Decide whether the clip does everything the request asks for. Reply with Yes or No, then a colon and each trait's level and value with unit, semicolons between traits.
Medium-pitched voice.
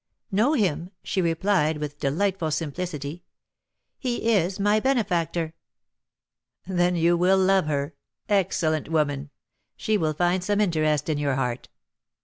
Yes: medium, 175 Hz